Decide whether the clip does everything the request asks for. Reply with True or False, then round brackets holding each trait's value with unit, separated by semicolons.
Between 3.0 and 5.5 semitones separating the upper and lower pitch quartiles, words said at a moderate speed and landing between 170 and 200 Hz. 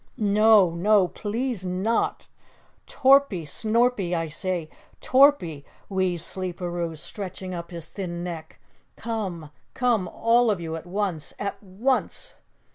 False (4.3 semitones; 120 wpm; 185 Hz)